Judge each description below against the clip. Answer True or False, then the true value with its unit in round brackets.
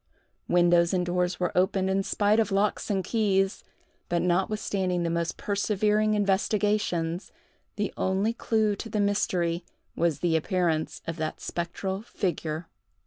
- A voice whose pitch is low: False (190 Hz)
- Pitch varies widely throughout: False (3.0 semitones)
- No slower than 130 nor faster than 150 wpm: True (140 wpm)